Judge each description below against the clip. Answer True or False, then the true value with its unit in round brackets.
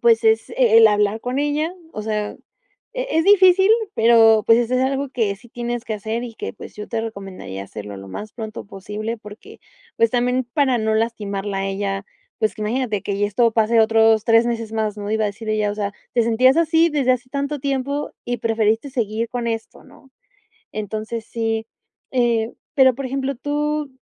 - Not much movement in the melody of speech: False (3.1 semitones)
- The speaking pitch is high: True (225 Hz)